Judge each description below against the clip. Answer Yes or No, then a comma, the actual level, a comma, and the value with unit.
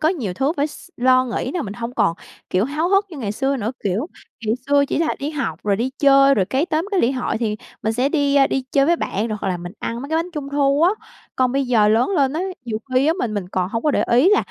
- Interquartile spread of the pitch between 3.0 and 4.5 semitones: No, average, 5.0 semitones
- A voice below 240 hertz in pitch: No, very high, 265 Hz